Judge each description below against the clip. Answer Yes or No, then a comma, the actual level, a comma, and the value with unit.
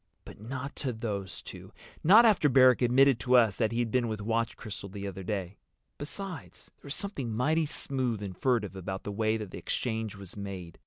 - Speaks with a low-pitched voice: Yes, low, 115 Hz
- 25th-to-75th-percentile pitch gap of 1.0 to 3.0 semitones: No, average, 4.5 semitones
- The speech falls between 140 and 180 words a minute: No, average, 195 wpm